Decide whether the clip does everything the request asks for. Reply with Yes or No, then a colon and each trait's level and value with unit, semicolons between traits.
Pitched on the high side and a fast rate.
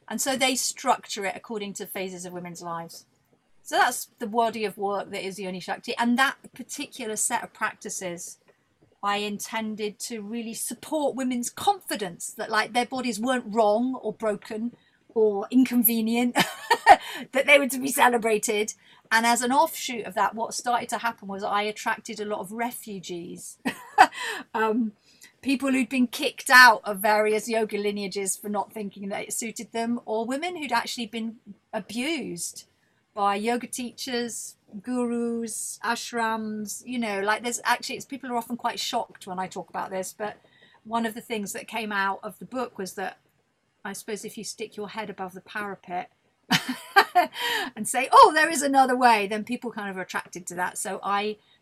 No: high, 225 Hz; average, 175 wpm